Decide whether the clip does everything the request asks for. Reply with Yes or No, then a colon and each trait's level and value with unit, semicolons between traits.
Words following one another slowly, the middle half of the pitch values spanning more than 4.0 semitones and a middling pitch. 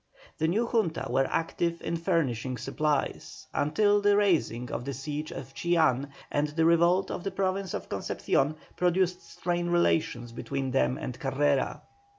No: average, 155 wpm; average, 4.7 semitones; medium, 160 Hz